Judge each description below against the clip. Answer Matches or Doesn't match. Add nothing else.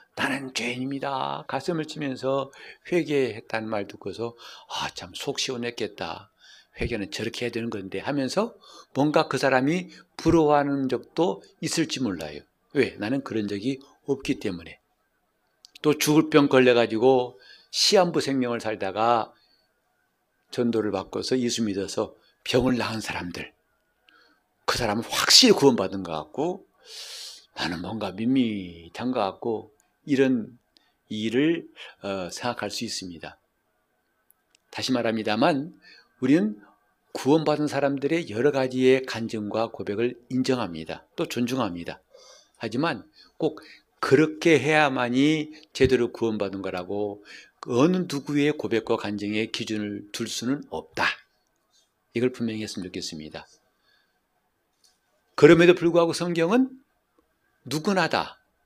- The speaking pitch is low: Matches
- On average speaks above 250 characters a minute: Matches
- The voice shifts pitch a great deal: Doesn't match